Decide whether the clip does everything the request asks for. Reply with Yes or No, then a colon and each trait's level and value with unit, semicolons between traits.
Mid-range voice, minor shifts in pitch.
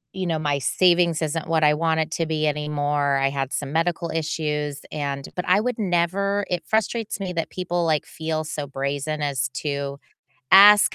No: medium, 155 Hz; average, 3.3 semitones